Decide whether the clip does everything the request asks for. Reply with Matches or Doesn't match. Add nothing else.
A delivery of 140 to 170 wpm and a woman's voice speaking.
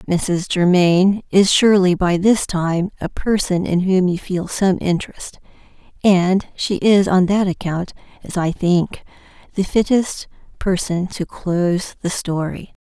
Matches